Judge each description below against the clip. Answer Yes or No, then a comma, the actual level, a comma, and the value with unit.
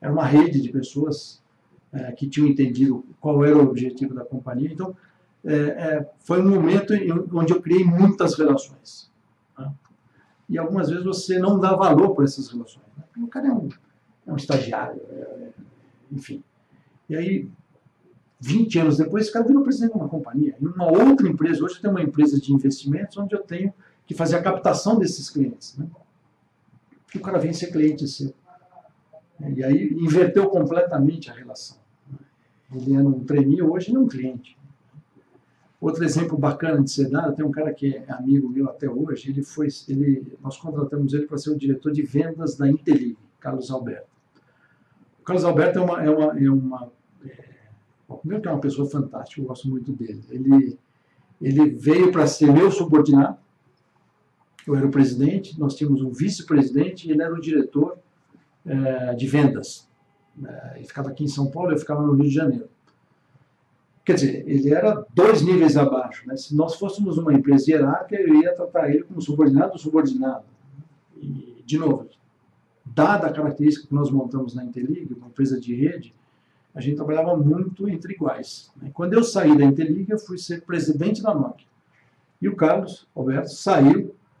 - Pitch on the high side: No, medium, 150 Hz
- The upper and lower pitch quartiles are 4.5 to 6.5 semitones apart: No, average, 3.8 semitones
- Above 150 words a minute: Yes, average, 175 wpm